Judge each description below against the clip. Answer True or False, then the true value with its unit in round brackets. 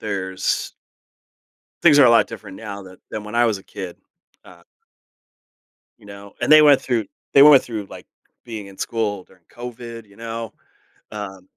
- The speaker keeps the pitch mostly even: False (3.1 semitones)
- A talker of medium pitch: False (105 Hz)